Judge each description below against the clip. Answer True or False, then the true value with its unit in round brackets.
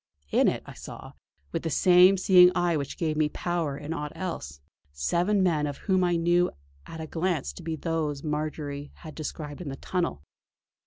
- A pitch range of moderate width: True (3.2 semitones)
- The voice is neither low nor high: True (160 Hz)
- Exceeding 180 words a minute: True (200 wpm)